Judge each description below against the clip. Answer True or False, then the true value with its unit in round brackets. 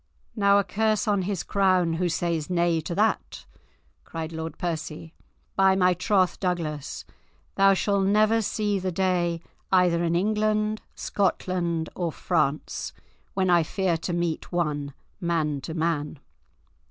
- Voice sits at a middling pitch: True (180 Hz)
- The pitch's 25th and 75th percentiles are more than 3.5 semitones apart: False (3.0 semitones)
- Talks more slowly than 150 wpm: True (140 wpm)